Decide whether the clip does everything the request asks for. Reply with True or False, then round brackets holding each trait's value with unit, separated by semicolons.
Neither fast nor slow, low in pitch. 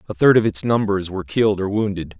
False (245 wpm; 100 Hz)